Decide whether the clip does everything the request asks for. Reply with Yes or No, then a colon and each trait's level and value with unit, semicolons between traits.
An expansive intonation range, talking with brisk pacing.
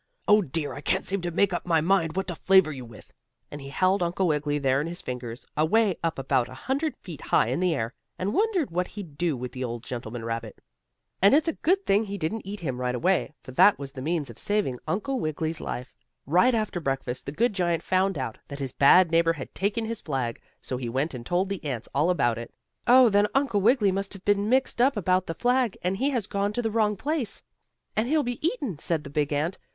Yes: wide, 6.9 semitones; fast, 240 wpm